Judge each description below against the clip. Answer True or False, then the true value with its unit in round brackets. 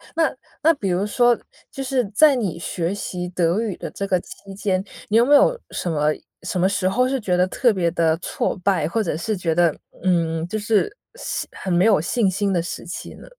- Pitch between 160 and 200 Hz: True (190 Hz)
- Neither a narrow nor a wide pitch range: True (4.6 semitones)